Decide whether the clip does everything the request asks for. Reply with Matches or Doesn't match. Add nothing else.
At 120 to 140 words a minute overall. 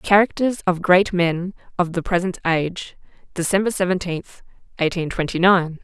Matches